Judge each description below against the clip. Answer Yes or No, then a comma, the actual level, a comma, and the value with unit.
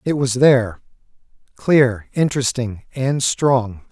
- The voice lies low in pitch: Yes, low, 125 Hz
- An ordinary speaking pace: No, slow, 90 wpm